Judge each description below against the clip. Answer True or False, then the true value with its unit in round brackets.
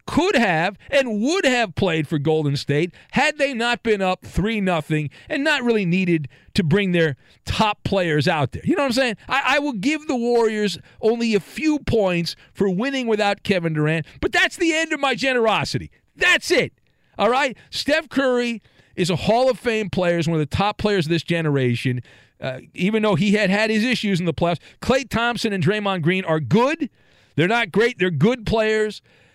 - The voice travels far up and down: True (6.1 semitones)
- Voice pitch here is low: False (205 Hz)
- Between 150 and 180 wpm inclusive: False (200 wpm)